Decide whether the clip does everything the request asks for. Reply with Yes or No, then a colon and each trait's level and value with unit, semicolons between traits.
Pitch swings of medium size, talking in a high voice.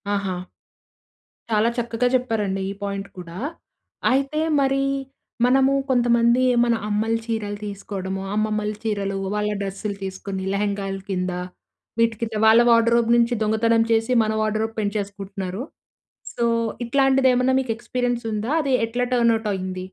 Yes: average, 3.0 semitones; high, 220 Hz